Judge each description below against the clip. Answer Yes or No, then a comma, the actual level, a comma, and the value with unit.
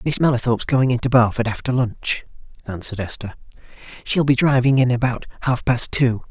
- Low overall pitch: Yes, low, 125 Hz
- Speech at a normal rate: Yes, average, 160 wpm